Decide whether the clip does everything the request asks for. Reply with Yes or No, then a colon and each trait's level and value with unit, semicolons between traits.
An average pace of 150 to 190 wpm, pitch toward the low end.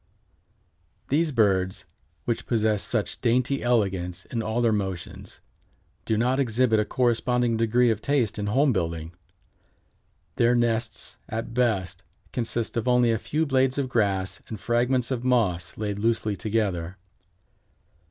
No: average, 140 wpm; low, 115 Hz